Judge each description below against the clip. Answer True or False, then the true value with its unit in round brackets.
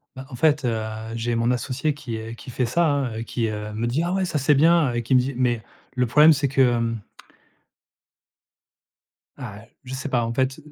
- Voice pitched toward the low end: True (125 Hz)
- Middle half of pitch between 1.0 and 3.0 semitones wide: False (3.5 semitones)